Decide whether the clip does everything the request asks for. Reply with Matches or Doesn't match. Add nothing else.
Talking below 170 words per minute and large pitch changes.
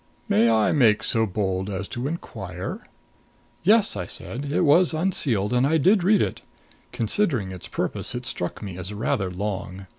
Doesn't match